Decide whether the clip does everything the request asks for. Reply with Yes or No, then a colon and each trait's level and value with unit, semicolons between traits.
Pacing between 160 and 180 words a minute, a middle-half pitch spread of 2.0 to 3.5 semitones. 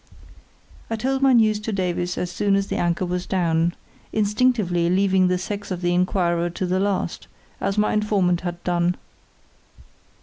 Yes: average, 165 wpm; average, 2.9 semitones